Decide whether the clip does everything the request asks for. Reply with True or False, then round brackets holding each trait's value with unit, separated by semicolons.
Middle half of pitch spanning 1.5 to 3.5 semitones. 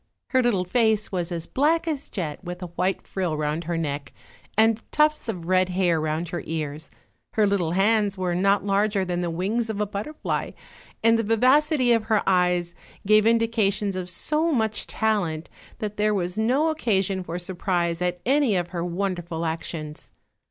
False (4.2 semitones)